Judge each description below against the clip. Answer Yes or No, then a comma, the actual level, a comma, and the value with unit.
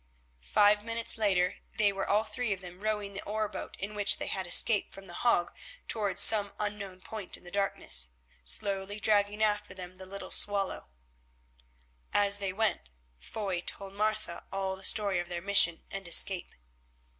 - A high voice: Yes, high, 200 Hz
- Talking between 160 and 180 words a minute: Yes, average, 175 wpm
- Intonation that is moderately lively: No, narrow, 2.0 semitones